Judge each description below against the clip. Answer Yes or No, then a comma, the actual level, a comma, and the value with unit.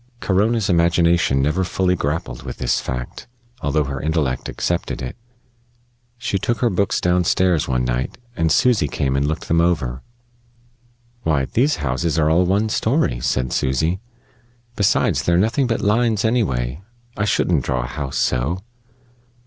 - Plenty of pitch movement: Yes, wide, 6.4 semitones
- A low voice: Yes, very low, 85 Hz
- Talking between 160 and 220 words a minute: No, average, 150 wpm